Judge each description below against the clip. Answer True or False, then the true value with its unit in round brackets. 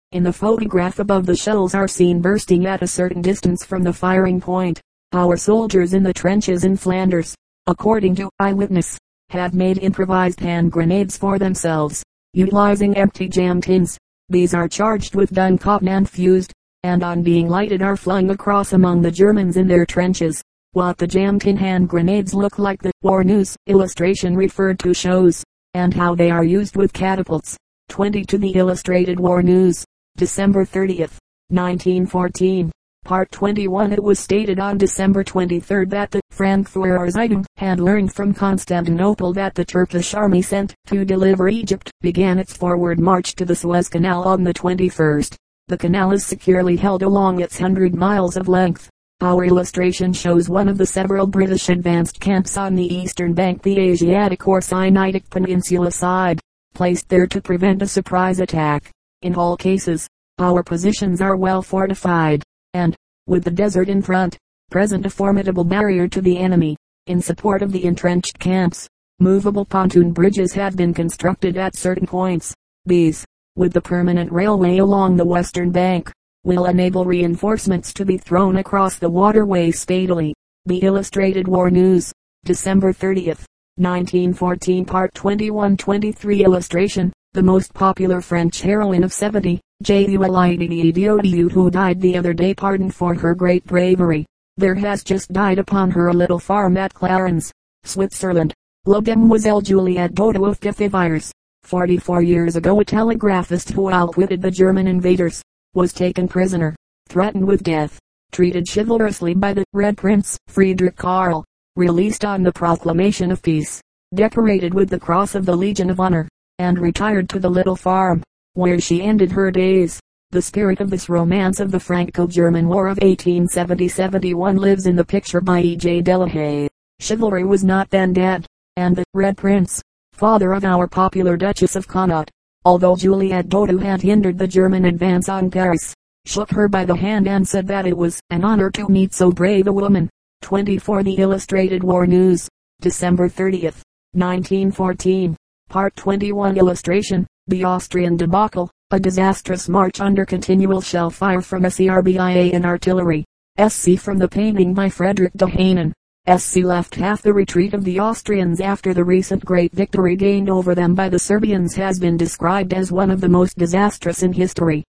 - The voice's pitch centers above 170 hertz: True (185 Hz)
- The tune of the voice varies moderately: False (1.6 semitones)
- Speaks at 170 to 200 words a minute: False (160 wpm)